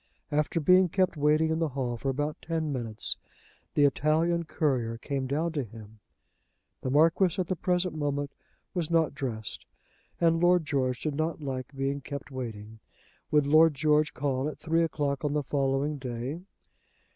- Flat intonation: No, average, 3.3 semitones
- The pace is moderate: Yes, average, 165 wpm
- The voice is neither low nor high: Yes, medium, 145 Hz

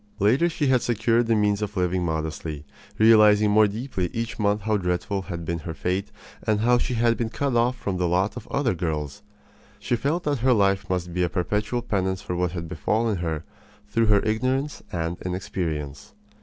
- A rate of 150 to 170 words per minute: No, average, 195 wpm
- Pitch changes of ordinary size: Yes, average, 4.5 semitones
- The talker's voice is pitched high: No, low, 105 Hz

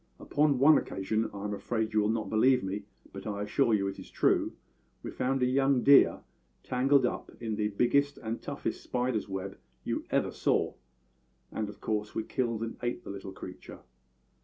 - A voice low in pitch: Yes, low, 110 Hz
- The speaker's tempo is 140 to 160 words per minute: No, average, 185 wpm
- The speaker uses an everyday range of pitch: Yes, average, 3.6 semitones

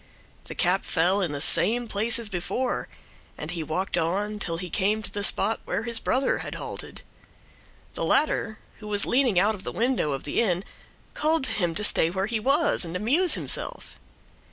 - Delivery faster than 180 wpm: Yes, average, 195 wpm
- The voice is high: Yes, high, 205 Hz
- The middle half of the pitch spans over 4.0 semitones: Yes, average, 4.7 semitones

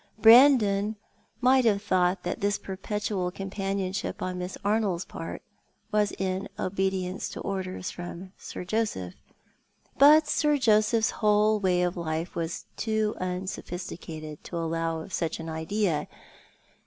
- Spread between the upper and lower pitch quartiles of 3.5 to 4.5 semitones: No, average, 3.0 semitones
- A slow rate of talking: Yes, slow, 130 wpm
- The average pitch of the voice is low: No, high, 190 Hz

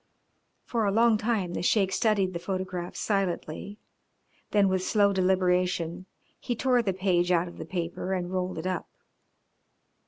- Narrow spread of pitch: Yes, narrow, 2.2 semitones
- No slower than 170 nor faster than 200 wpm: No, average, 155 wpm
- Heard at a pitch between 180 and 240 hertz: Yes, medium, 185 Hz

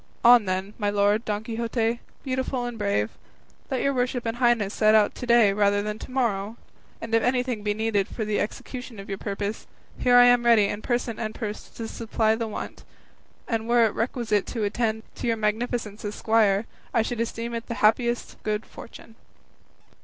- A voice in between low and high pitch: No, high, 225 Hz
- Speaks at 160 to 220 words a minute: Yes, average, 190 wpm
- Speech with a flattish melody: Yes, narrow, 2.3 semitones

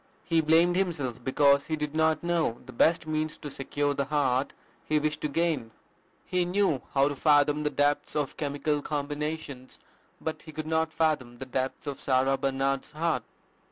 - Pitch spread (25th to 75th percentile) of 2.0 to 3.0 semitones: Yes, narrow, 2.5 semitones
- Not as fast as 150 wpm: No, average, 175 wpm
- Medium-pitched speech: Yes, medium, 150 Hz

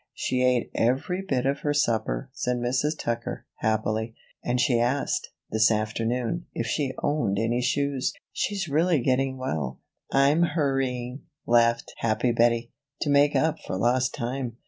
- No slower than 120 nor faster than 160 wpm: Yes, average, 145 wpm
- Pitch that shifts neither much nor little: Yes, average, 3.2 semitones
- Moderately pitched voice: No, low, 125 Hz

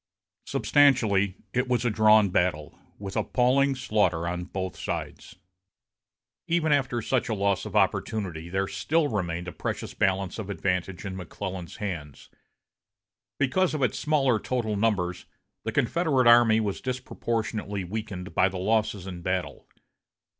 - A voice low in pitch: Yes, low, 105 Hz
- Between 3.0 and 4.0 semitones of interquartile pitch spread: No, average, 4.9 semitones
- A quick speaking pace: No, average, 140 wpm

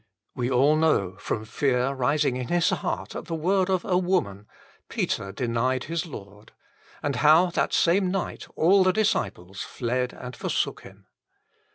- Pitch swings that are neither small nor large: No, wide, 6.4 semitones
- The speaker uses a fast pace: No, average, 165 wpm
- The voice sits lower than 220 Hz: Yes, medium, 140 Hz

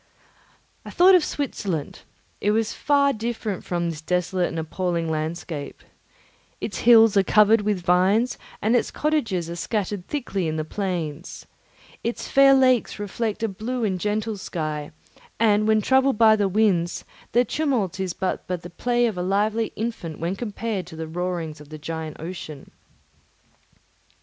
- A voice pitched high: Yes, high, 200 Hz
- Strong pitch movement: No, average, 4.8 semitones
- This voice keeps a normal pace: Yes, average, 160 wpm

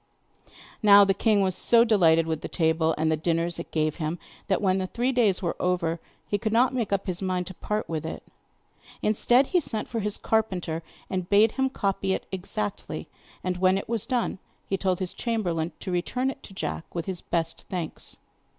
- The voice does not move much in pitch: No, average, 4.2 semitones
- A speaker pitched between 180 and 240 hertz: Yes, high, 190 Hz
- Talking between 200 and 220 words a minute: Yes, fast, 205 wpm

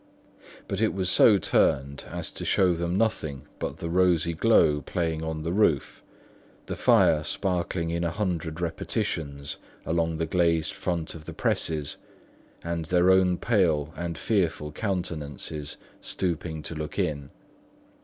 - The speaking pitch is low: Yes, very low, 85 Hz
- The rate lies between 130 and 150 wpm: Yes, average, 145 wpm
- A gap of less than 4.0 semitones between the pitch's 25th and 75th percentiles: Yes, narrow, 2.6 semitones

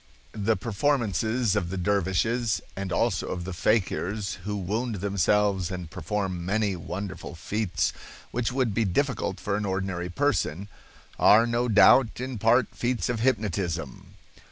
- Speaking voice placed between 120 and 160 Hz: No, low, 100 Hz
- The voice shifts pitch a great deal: No, average, 3.8 semitones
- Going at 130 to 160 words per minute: Yes, average, 140 wpm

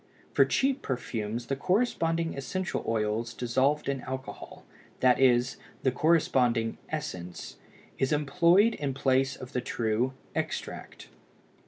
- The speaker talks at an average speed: No, slow, 120 wpm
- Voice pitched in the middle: No, low, 130 Hz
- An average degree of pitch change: Yes, average, 4.3 semitones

